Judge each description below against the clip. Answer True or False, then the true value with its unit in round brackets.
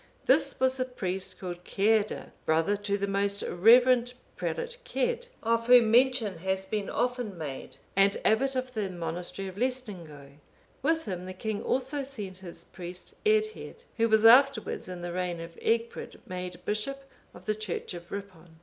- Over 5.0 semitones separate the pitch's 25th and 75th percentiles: True (5.5 semitones)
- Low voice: False (205 Hz)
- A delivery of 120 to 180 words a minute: True (165 wpm)